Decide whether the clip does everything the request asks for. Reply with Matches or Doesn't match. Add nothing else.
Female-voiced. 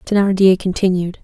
Matches